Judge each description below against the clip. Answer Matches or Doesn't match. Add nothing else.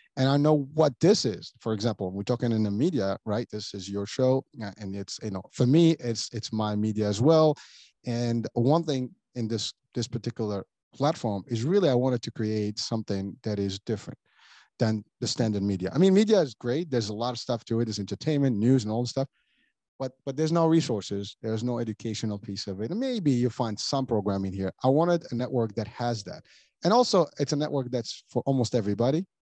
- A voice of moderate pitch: Doesn't match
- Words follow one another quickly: Matches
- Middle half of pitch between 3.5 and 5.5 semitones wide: Matches